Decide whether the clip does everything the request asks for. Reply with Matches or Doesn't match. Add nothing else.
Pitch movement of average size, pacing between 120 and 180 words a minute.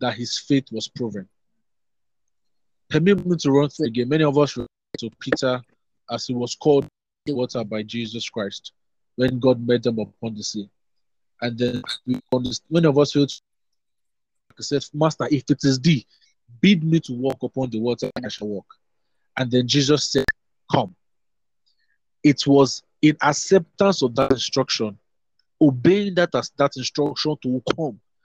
Matches